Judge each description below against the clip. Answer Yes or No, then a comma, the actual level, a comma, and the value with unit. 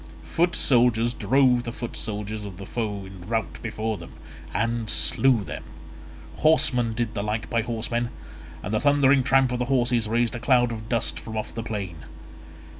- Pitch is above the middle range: No, low, 115 Hz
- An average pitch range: No, narrow, 2.3 semitones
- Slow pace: No, average, 180 wpm